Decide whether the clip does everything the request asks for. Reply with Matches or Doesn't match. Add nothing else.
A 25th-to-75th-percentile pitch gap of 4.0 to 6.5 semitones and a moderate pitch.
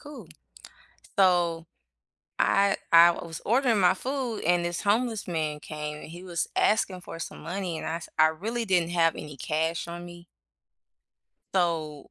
Doesn't match